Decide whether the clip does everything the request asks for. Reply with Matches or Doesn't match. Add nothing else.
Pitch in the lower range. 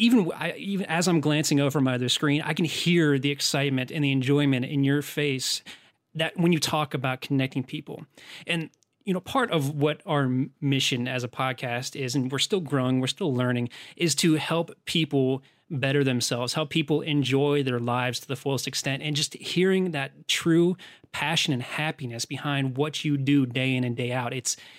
Doesn't match